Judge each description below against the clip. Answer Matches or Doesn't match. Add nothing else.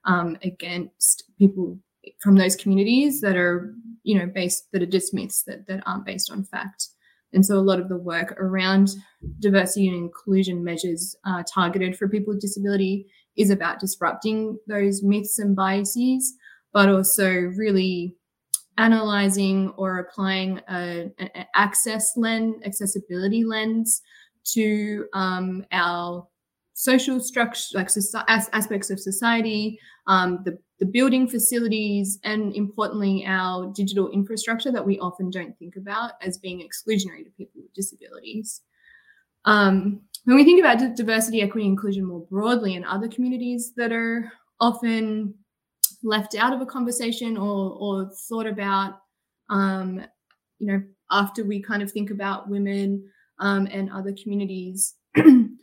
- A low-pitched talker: Doesn't match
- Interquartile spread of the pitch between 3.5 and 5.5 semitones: Doesn't match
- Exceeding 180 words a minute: Doesn't match